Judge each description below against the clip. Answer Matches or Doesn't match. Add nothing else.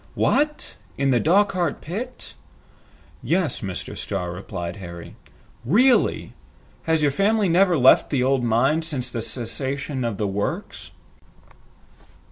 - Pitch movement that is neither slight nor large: Doesn't match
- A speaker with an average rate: Doesn't match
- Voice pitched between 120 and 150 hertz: Matches